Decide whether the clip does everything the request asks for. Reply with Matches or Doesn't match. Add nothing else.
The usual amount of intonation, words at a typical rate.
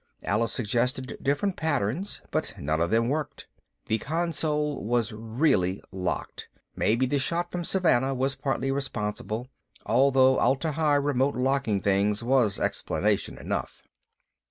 Doesn't match